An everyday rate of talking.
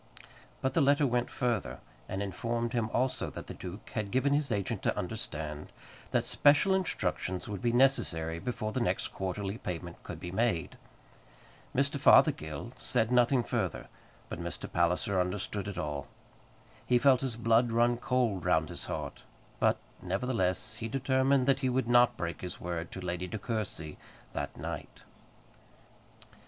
Yes: average, 155 wpm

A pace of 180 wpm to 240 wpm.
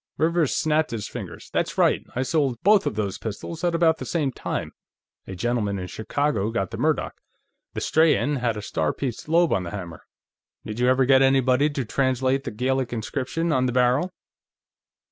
Yes: average, 185 wpm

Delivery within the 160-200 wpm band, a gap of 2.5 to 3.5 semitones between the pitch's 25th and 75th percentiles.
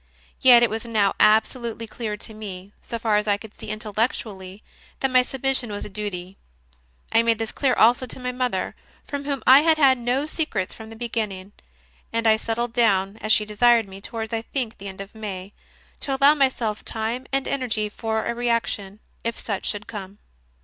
Yes: average, 195 wpm; average, 2.9 semitones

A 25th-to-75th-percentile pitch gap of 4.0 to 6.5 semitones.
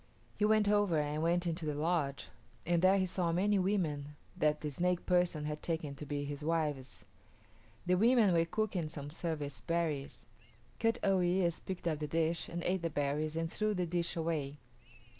No: average, 3.2 semitones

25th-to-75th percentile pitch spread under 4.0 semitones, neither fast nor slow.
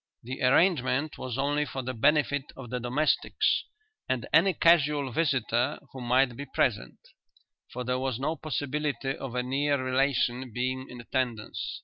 Yes: narrow, 2.5 semitones; average, 150 wpm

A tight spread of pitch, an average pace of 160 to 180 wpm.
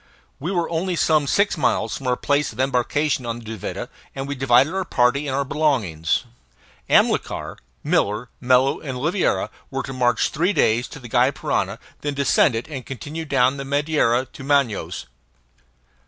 No: average, 3.3 semitones; average, 175 wpm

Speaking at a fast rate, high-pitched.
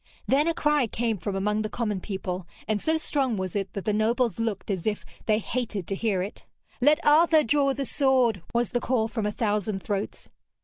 Yes: fast, 210 wpm; high, 220 Hz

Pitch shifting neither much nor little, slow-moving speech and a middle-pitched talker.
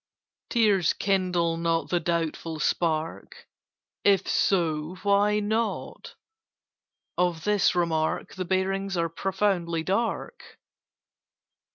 Yes: average, 3.1 semitones; slow, 90 wpm; medium, 180 Hz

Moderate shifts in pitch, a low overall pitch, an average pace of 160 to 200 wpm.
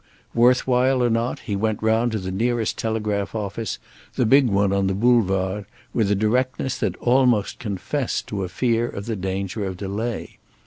Yes: average, 3.5 semitones; low, 110 Hz; average, 180 wpm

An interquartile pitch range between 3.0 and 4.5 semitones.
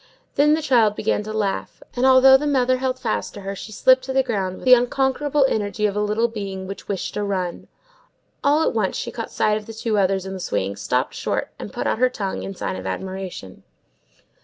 No: average, 4.9 semitones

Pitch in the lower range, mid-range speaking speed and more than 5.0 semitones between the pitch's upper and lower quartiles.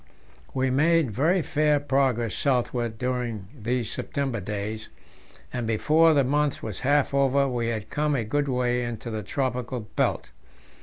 No: low, 125 Hz; average, 150 wpm; average, 3.5 semitones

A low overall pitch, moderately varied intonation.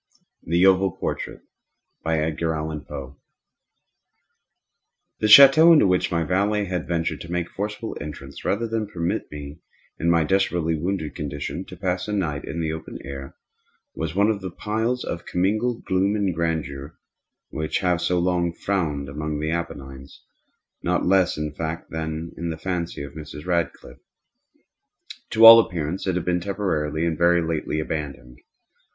Yes: very low, 85 Hz; average, 3.6 semitones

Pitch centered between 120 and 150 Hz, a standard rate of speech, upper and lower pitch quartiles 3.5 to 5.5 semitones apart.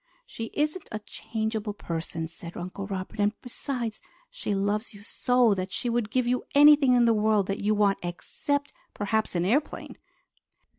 No: high, 215 Hz; average, 165 wpm; average, 3.8 semitones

